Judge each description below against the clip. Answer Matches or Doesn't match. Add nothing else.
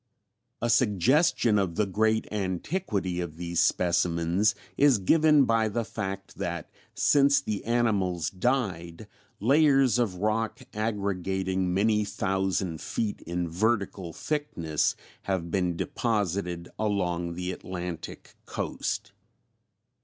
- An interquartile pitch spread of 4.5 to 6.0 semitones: Doesn't match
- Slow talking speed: Matches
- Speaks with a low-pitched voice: Matches